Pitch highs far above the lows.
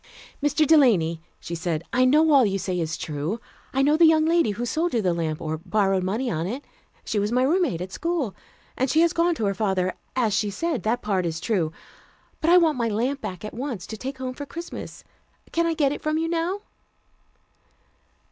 Yes: wide, 8.6 semitones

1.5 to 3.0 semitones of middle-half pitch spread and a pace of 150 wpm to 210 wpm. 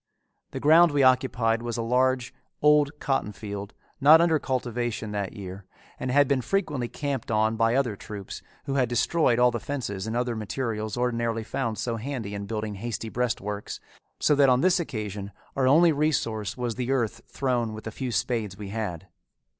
No: average, 3.7 semitones; average, 180 wpm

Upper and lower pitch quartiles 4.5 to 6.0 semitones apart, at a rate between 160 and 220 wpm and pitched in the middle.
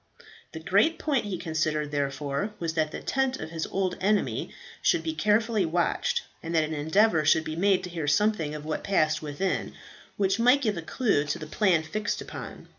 Yes: average, 5.1 semitones; average, 195 wpm; medium, 175 Hz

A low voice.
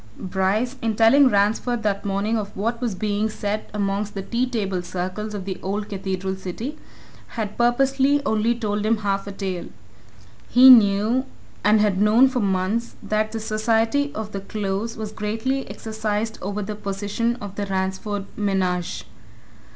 No: high, 210 Hz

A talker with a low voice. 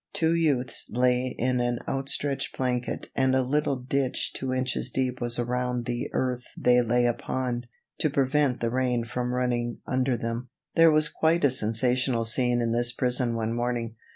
Yes: low, 125 Hz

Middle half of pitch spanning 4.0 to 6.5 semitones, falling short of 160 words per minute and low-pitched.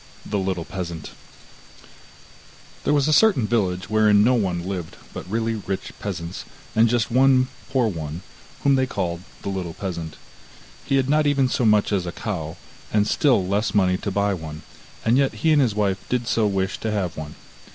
No: average, 4.9 semitones; average, 185 wpm; low, 105 Hz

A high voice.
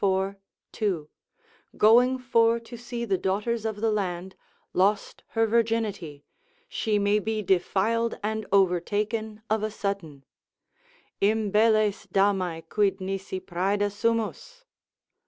Yes: high, 210 Hz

